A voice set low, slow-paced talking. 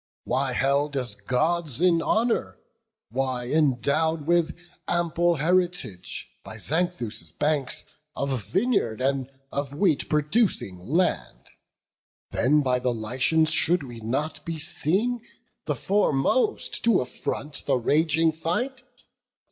No: medium, 150 Hz; slow, 115 wpm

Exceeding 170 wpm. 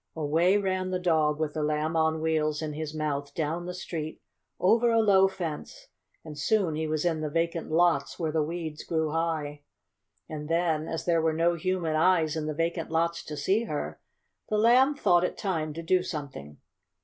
Yes: average, 195 wpm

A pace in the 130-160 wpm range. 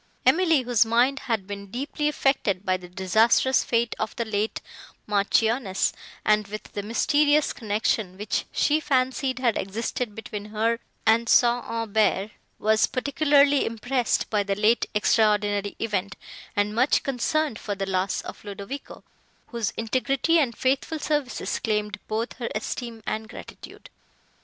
Yes: average, 140 wpm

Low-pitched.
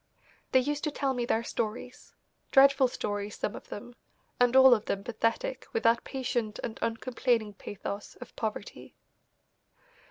No: high, 240 Hz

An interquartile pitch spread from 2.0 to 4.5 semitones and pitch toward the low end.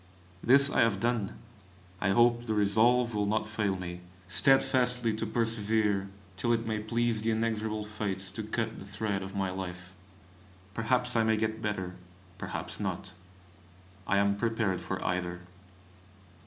Yes: average, 2.7 semitones; low, 110 Hz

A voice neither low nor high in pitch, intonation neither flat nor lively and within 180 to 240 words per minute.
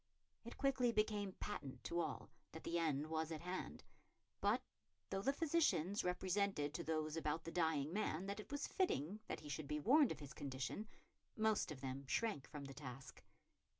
No: medium, 165 Hz; wide, 5.9 semitones; average, 185 wpm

